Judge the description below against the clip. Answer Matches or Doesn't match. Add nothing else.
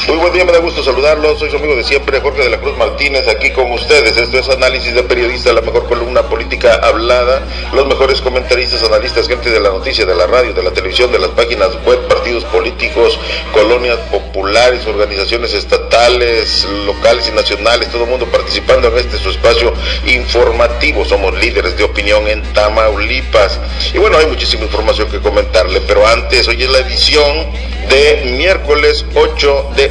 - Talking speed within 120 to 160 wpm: Doesn't match